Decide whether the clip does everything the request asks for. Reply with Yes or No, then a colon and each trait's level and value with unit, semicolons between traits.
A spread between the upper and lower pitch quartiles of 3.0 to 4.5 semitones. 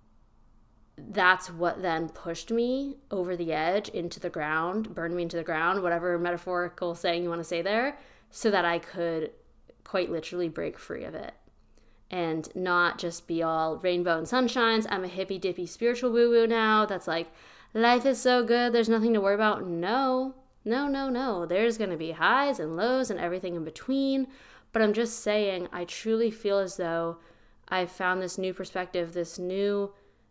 No: average, 5.1 semitones